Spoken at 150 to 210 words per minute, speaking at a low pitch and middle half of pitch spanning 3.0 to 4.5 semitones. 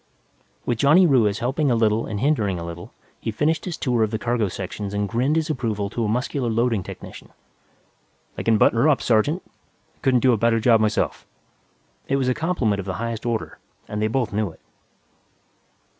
Yes: average, 200 wpm; low, 115 Hz; average, 3.7 semitones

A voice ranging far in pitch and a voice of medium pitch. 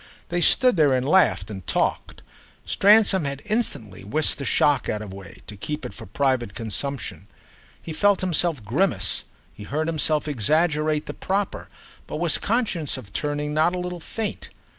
Yes: wide, 7.8 semitones; medium, 150 Hz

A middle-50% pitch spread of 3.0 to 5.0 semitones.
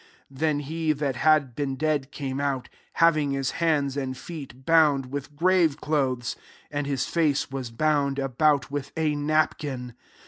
No: narrow, 2.4 semitones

